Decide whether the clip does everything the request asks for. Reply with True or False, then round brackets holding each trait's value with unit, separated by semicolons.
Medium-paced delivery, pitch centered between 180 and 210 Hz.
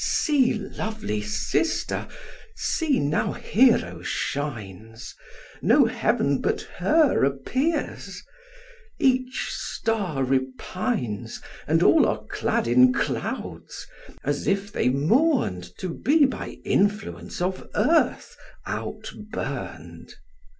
False (95 wpm; 185 Hz)